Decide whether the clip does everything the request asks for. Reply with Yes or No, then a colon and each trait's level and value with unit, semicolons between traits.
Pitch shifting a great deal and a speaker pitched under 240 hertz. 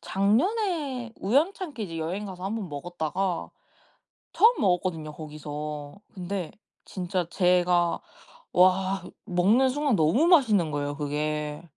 Yes: wide, 5.9 semitones; medium, 185 Hz